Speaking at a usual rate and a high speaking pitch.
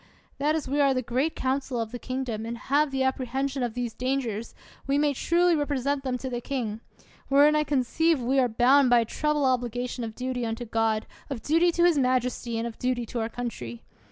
No: fast, 215 wpm; very high, 255 Hz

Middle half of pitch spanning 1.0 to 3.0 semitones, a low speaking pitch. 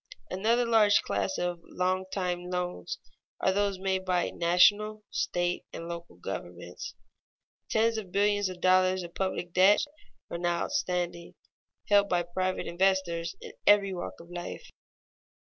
No: narrow, 2.4 semitones; medium, 185 Hz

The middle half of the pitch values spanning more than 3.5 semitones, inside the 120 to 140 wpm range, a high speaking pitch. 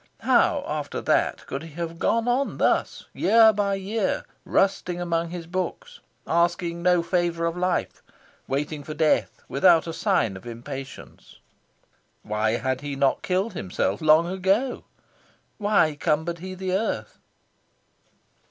No: average, 3.9 semitones; slow, 135 wpm; medium, 170 Hz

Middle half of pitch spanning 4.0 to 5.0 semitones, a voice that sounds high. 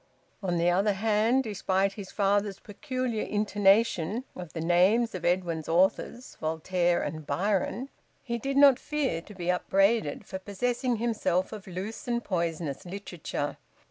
Yes: average, 4.3 semitones; high, 195 Hz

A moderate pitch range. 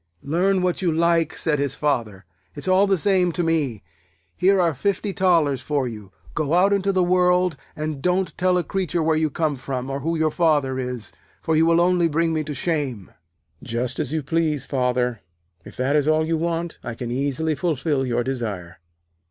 Yes: average, 4.7 semitones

